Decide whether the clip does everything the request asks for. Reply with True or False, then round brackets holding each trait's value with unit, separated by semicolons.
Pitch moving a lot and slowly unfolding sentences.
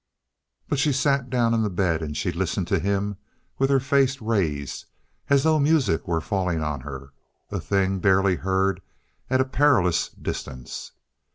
False (7.5 semitones; 165 wpm)